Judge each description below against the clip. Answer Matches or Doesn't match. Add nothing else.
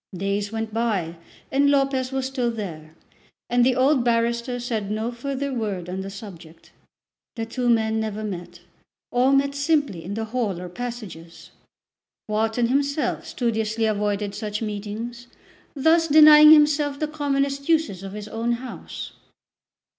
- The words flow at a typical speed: Matches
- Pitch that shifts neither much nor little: Matches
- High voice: Matches